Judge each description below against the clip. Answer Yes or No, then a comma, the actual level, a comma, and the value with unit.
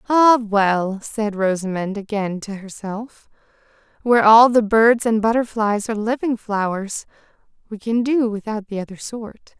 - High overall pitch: Yes, high, 220 Hz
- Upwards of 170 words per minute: No, average, 145 wpm